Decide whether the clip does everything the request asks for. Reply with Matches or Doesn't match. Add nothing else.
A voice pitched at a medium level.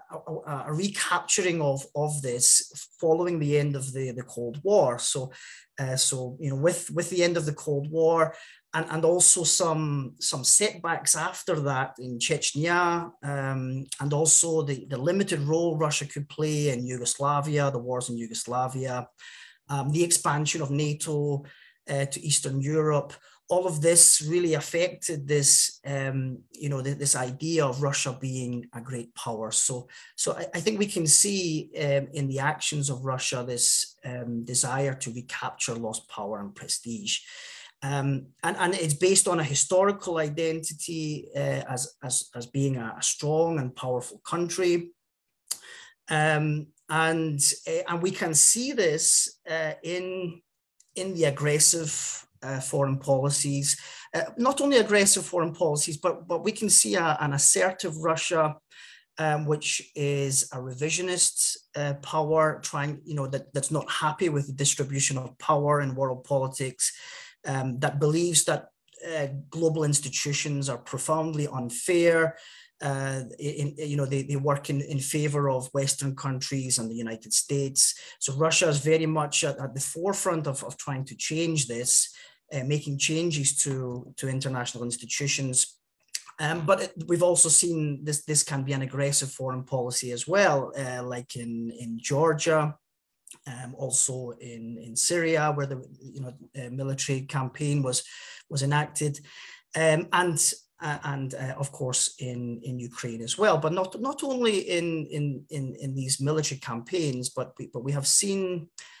Matches